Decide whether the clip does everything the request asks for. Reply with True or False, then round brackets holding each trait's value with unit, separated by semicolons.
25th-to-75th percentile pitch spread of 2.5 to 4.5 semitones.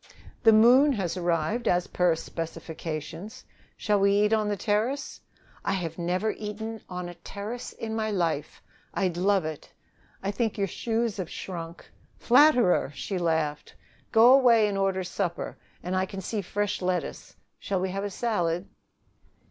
True (3.9 semitones)